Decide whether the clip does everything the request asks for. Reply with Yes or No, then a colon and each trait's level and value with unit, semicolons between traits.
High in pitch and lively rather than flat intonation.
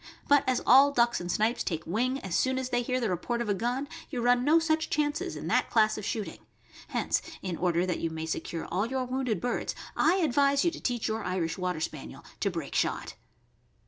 Yes: high, 240 Hz; wide, 6.3 semitones